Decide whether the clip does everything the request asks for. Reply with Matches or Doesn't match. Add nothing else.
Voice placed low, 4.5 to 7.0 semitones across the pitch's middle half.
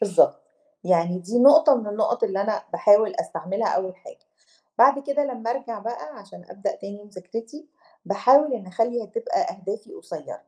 Doesn't match